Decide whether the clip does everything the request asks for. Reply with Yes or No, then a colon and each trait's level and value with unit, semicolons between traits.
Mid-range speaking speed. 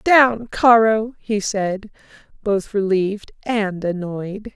No: slow, 105 wpm